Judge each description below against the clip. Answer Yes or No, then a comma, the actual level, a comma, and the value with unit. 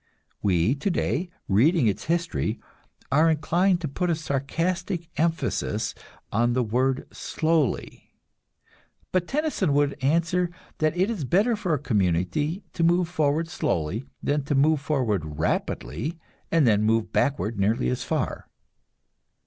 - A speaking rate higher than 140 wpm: No, slow, 135 wpm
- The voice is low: No, medium, 150 Hz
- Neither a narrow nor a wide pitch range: No, wide, 6.3 semitones